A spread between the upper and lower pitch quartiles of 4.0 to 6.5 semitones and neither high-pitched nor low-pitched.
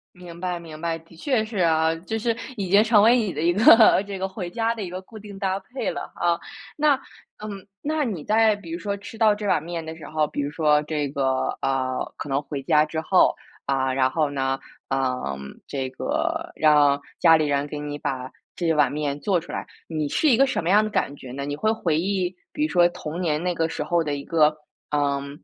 Yes: wide, 5.5 semitones; medium, 165 Hz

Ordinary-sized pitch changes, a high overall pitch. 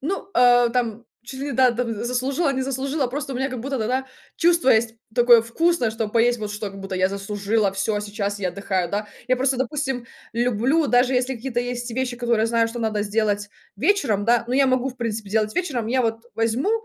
Yes: average, 3.2 semitones; high, 240 Hz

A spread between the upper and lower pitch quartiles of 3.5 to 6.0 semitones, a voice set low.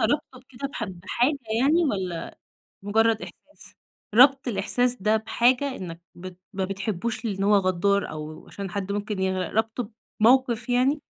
No: average, 4.6 semitones; high, 220 Hz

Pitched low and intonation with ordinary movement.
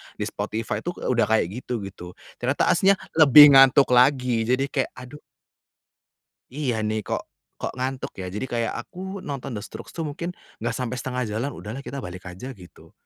Yes: low, 125 Hz; average, 3.9 semitones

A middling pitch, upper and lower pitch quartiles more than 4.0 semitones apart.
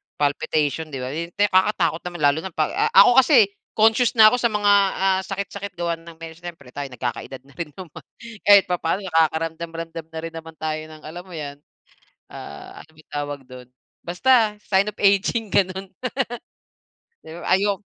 Yes: medium, 170 Hz; average, 4.4 semitones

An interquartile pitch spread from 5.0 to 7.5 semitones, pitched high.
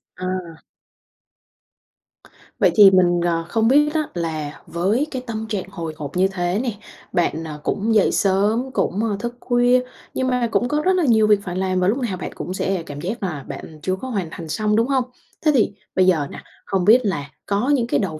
Yes: average, 5.3 semitones; high, 195 Hz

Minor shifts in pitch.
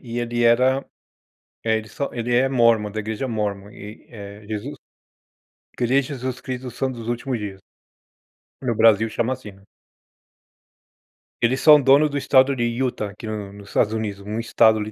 No: average, 3.4 semitones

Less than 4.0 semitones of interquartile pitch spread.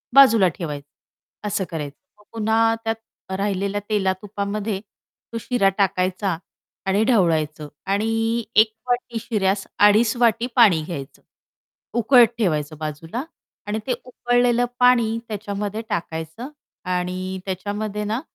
Yes: average, 3.5 semitones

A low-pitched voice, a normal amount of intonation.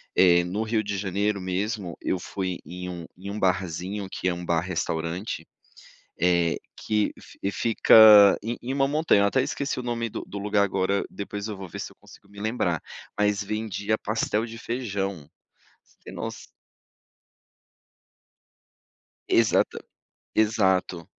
Yes: low, 100 Hz; average, 3.0 semitones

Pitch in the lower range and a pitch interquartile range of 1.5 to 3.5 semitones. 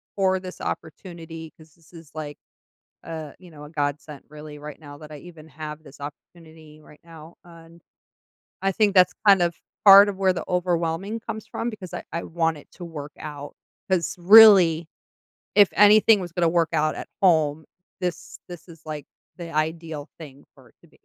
No: medium, 165 Hz; average, 2.9 semitones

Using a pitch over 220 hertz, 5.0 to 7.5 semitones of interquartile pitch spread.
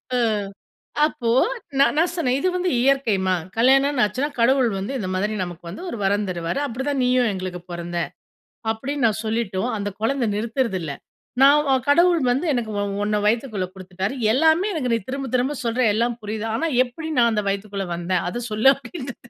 Yes: high, 235 Hz; average, 5.3 semitones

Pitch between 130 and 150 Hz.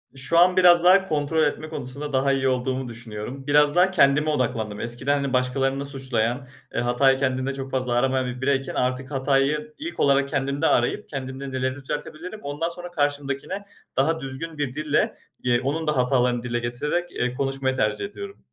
Yes: low, 135 Hz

